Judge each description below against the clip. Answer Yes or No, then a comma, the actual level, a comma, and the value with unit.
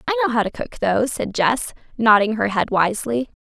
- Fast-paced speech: Yes, fast, 210 wpm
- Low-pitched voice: No, high, 235 Hz